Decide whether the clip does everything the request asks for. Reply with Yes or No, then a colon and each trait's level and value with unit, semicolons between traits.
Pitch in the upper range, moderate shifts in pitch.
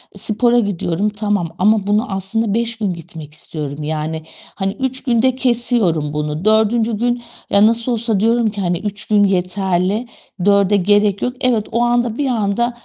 Yes: high, 210 Hz; average, 3.9 semitones